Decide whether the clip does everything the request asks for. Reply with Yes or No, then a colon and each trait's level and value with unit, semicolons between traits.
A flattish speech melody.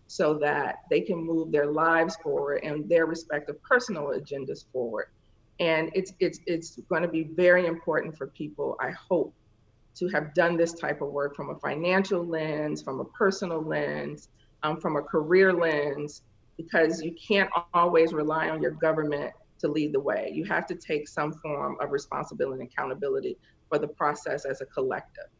No: average, 3.1 semitones